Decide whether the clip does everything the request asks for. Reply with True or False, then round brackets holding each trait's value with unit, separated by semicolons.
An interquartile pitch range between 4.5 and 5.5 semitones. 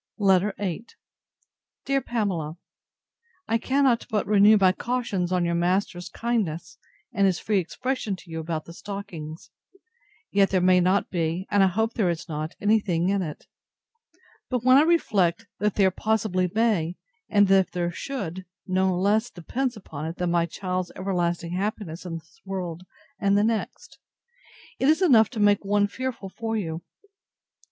False (3.8 semitones)